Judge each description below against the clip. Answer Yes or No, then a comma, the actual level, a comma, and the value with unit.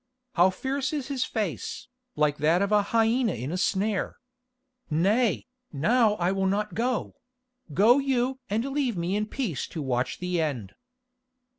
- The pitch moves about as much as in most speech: No, wide, 6.4 semitones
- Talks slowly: No, average, 150 wpm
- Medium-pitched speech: No, high, 210 Hz